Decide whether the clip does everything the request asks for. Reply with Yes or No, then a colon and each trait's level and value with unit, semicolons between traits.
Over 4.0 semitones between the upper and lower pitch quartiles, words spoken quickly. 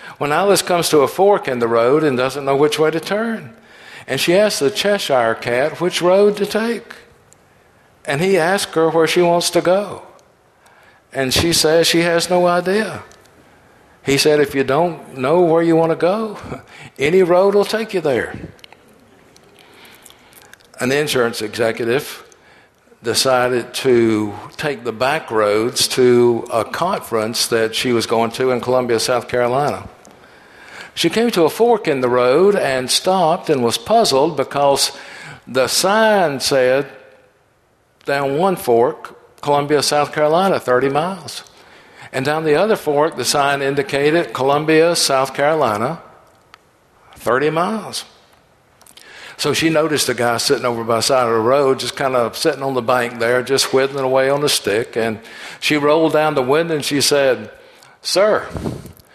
No: average, 5.3 semitones; average, 155 wpm